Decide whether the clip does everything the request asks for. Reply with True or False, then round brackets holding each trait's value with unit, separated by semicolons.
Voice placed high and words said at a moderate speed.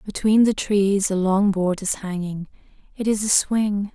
True (200 Hz; 165 wpm)